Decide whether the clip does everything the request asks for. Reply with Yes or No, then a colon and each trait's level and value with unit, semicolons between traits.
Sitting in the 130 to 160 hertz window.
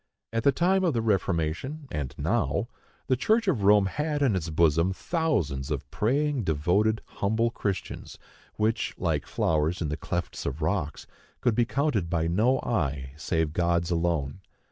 No: very low, 95 Hz